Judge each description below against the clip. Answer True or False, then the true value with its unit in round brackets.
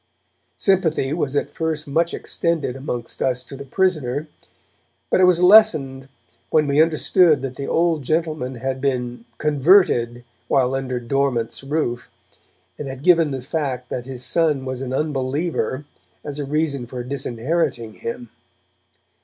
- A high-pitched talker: False (140 Hz)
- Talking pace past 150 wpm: False (145 wpm)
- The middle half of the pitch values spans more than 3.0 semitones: True (3.8 semitones)